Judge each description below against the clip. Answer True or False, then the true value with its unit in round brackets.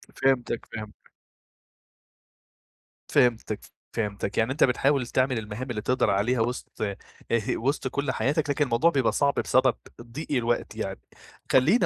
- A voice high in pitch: False (125 Hz)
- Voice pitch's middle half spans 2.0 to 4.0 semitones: True (3.3 semitones)